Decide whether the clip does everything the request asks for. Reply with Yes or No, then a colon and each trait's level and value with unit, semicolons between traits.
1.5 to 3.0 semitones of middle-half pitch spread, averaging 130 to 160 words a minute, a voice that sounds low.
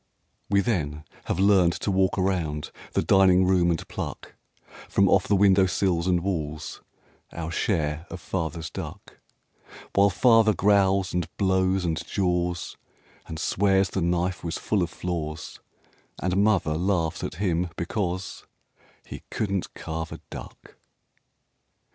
Yes: narrow, 2.5 semitones; slow, 135 wpm; very low, 90 Hz